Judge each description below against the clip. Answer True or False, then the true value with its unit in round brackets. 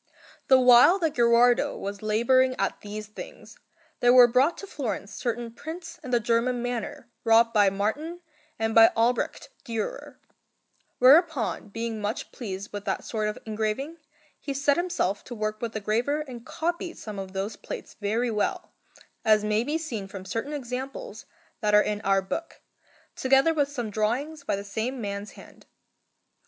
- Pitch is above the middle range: True (235 Hz)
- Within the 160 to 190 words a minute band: True (165 wpm)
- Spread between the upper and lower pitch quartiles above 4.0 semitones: True (4.4 semitones)